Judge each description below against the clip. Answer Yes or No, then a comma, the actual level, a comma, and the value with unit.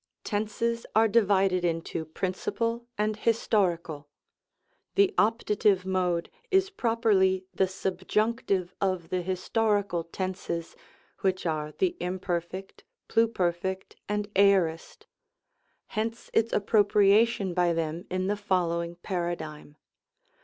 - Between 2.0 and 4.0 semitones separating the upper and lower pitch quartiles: Yes, average, 3.5 semitones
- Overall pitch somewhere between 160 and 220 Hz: Yes, high, 190 Hz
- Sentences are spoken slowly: Yes, slow, 105 wpm